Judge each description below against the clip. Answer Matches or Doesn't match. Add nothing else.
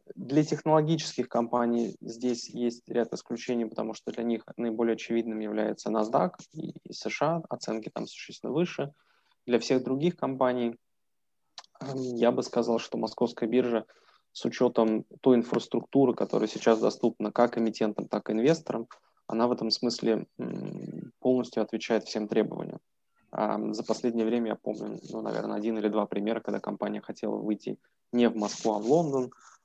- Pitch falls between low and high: Doesn't match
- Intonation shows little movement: Matches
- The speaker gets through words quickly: Doesn't match